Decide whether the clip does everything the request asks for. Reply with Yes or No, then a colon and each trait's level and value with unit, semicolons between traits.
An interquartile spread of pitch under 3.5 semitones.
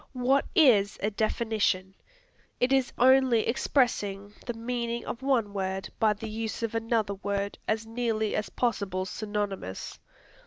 Yes: average, 3.0 semitones